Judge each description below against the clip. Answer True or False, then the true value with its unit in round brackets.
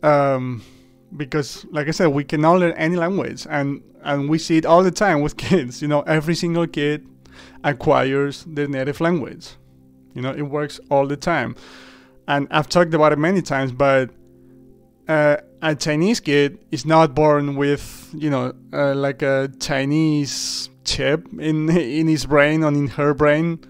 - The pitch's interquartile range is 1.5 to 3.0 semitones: True (2.5 semitones)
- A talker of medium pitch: True (150 Hz)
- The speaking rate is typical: True (170 wpm)